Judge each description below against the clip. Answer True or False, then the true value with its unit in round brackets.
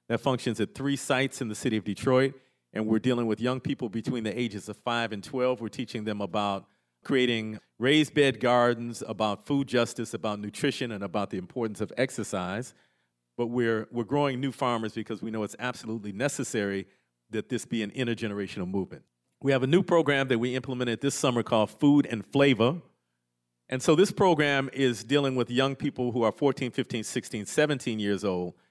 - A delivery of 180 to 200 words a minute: True (190 wpm)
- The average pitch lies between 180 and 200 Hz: False (120 Hz)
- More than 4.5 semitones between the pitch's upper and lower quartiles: False (3.7 semitones)